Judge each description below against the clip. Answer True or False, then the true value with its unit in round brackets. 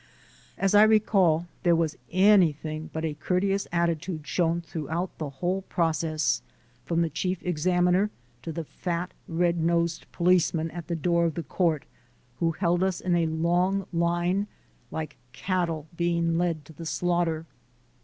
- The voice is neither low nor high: True (170 Hz)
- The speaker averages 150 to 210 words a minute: True (155 wpm)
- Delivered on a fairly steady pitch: True (1.9 semitones)